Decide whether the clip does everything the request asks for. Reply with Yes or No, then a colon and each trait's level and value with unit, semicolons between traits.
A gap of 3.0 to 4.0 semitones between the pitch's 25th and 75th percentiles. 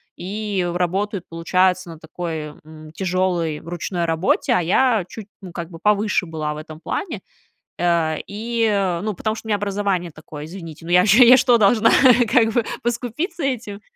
No: average, 4.4 semitones